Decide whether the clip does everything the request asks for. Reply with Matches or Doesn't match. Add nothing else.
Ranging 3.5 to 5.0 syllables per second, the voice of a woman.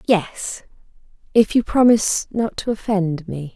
Matches